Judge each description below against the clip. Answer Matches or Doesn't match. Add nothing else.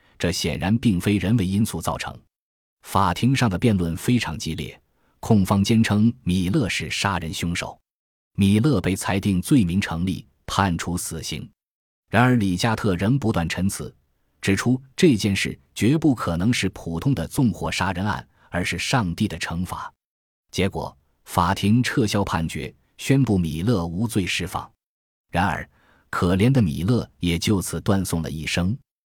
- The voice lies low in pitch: Matches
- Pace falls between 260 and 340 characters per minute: Doesn't match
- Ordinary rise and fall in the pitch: Matches